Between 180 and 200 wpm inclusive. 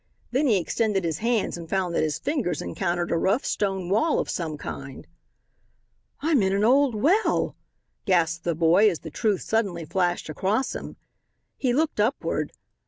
No: average, 170 wpm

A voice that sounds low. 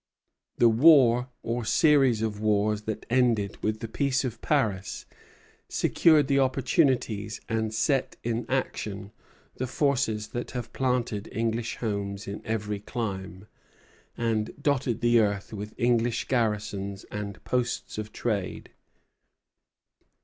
Yes: low, 115 Hz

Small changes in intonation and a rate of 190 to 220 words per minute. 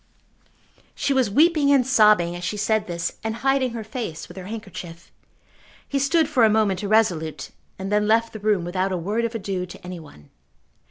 No: average, 4.3 semitones; average, 195 wpm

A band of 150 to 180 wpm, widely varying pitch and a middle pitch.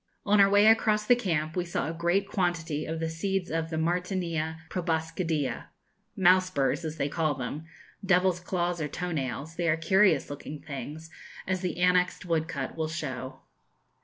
No: average, 170 wpm; narrow, 2.6 semitones; medium, 165 Hz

